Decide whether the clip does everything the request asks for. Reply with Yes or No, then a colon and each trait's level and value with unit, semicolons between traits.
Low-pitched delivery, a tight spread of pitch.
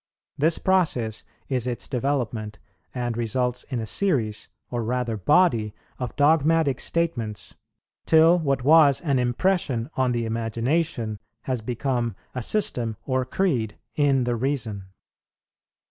No: low, 125 Hz; average, 4.2 semitones